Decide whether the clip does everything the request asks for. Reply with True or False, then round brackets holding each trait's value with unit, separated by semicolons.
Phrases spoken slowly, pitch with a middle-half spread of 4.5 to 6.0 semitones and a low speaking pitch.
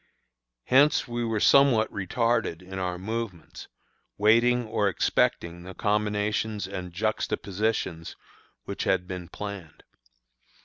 False (105 wpm; 3.5 semitones; 105 Hz)